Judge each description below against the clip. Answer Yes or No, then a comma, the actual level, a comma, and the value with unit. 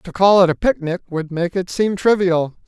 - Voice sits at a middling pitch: Yes, medium, 180 Hz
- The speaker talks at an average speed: No, fast, 225 wpm